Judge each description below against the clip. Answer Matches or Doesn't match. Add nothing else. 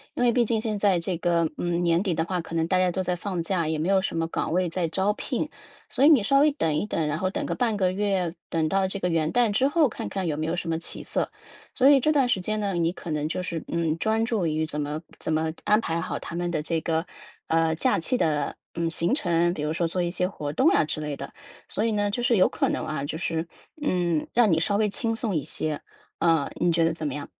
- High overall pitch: Doesn't match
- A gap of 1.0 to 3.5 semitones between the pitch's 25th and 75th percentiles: Doesn't match